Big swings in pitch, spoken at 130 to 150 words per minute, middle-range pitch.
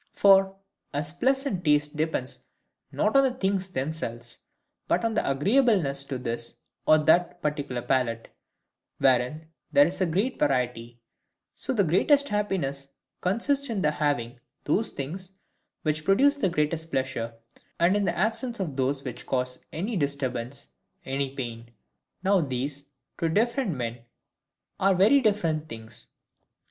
Yes: wide, 6.7 semitones; slow, 135 wpm; medium, 155 Hz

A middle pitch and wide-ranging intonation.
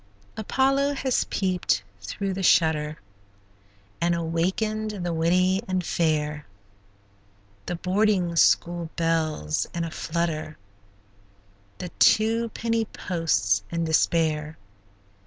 No: medium, 170 Hz; average, 3.6 semitones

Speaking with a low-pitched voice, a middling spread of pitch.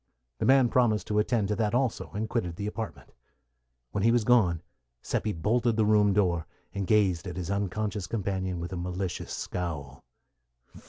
Yes: low, 100 Hz; average, 3.5 semitones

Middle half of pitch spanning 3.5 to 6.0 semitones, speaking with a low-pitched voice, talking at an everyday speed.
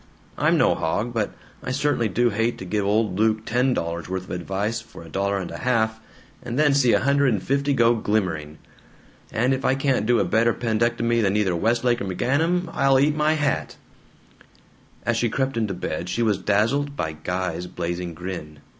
Yes: wide, 5.4 semitones; low, 110 Hz; average, 195 wpm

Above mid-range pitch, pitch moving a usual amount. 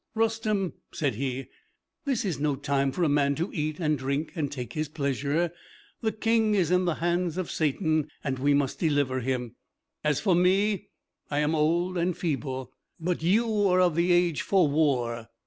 No: medium, 155 Hz; average, 4.3 semitones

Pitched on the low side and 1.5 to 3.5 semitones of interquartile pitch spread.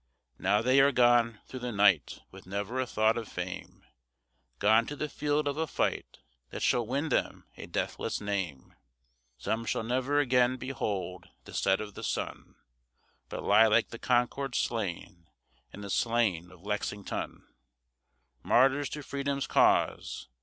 No: low, 115 Hz; average, 4.3 semitones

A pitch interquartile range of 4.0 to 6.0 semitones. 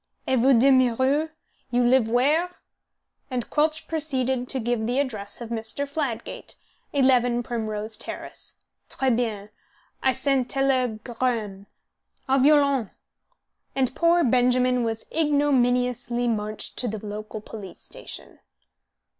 No: average, 3.1 semitones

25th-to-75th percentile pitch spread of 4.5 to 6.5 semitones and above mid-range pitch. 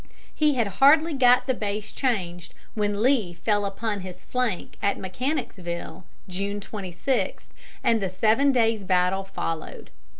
Yes: average, 5.0 semitones; high, 205 Hz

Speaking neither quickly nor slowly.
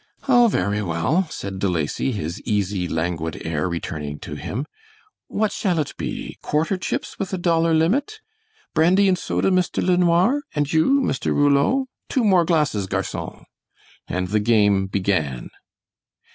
Yes: average, 145 wpm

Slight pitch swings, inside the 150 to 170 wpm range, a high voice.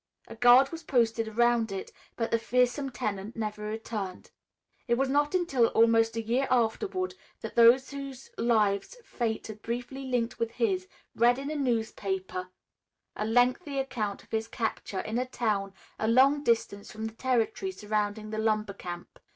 No: average, 3.0 semitones; average, 165 wpm; high, 230 Hz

